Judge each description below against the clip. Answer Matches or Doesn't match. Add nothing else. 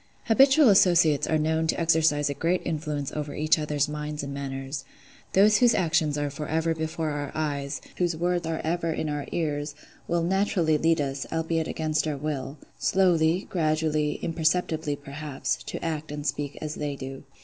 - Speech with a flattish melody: Matches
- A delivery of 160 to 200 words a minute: Matches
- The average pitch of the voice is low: Doesn't match